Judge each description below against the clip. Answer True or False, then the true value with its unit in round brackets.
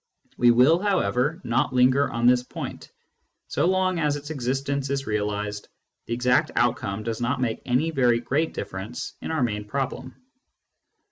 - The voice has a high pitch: False (125 Hz)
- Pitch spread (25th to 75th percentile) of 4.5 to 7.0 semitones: False (3.3 semitones)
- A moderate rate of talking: True (155 wpm)